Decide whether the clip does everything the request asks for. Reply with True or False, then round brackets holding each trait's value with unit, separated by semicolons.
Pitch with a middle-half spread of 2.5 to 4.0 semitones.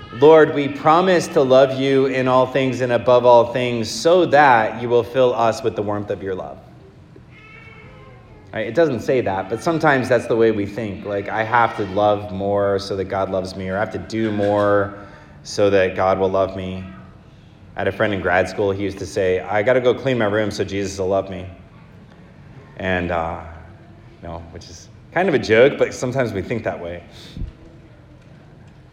False (5.0 semitones)